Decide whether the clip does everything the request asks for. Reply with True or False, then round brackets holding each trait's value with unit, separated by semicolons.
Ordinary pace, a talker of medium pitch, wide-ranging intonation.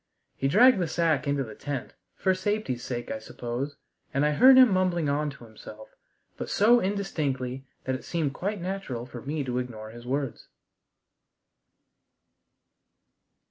True (150 wpm; 145 Hz; 6.9 semitones)